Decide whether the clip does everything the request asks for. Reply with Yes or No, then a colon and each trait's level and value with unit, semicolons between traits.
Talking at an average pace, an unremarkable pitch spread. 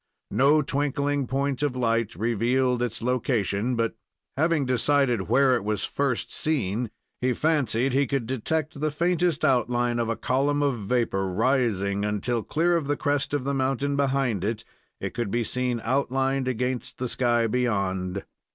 Yes: average, 160 wpm; average, 3.5 semitones